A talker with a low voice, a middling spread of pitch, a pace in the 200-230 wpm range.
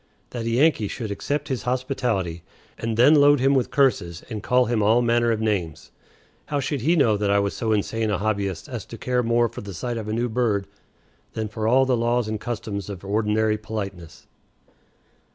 Yes: low, 110 Hz; average, 3.2 semitones; fast, 205 wpm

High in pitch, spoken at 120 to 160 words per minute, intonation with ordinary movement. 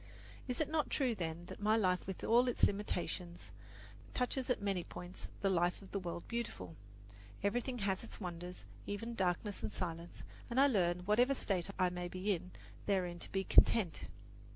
No: high, 195 Hz; average, 175 wpm; average, 4.4 semitones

